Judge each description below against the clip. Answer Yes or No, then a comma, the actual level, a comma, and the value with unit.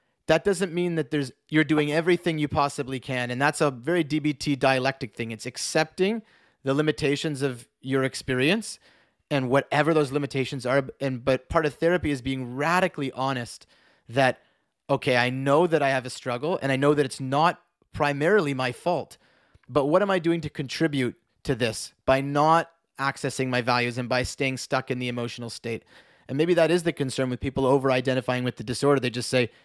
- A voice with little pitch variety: No, average, 3.4 semitones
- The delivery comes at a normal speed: Yes, average, 190 wpm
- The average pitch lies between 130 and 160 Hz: Yes, medium, 140 Hz